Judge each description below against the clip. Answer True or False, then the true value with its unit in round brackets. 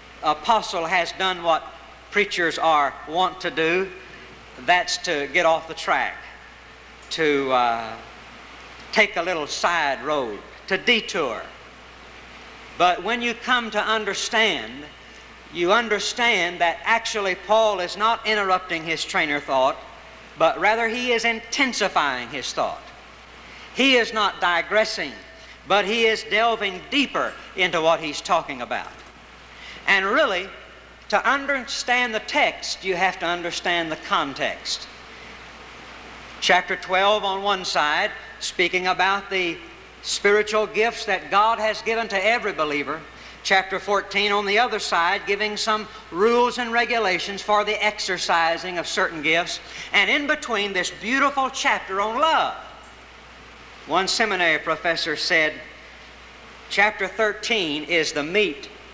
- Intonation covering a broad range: False (4.3 semitones)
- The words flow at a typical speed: False (125 wpm)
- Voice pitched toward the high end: True (195 Hz)